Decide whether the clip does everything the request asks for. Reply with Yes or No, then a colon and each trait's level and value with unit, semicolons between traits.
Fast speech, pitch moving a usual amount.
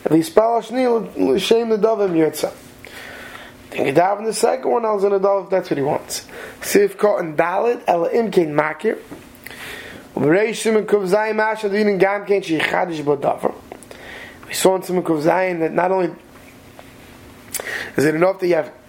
No: average, 150 wpm; average, 4.2 semitones